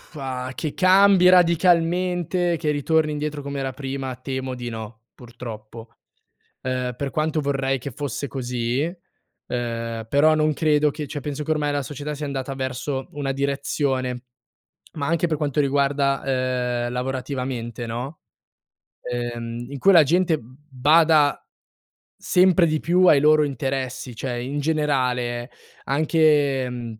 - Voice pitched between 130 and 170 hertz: Yes, medium, 140 Hz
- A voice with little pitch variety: No, average, 3.3 semitones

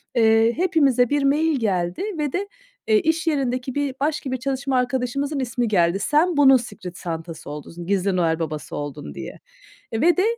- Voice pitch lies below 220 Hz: No, very high, 255 Hz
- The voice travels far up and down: Yes, wide, 7.4 semitones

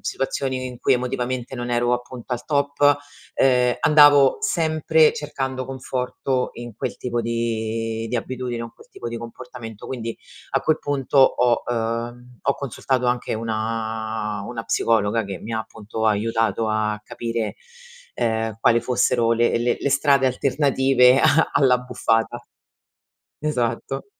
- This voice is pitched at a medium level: No, low, 120 Hz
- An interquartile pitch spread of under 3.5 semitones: Yes, average, 2.7 semitones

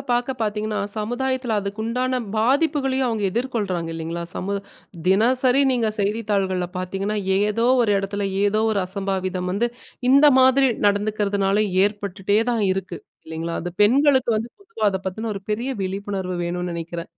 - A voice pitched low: No, high, 210 Hz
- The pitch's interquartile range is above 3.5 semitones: Yes, average, 4.0 semitones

